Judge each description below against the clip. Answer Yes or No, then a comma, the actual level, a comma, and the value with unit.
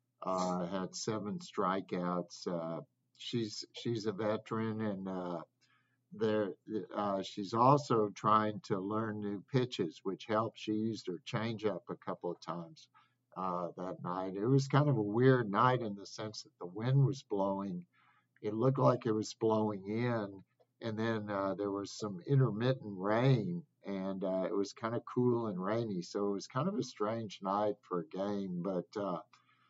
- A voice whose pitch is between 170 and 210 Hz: No, low, 110 Hz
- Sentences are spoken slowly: No, average, 175 wpm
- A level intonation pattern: No, average, 4.0 semitones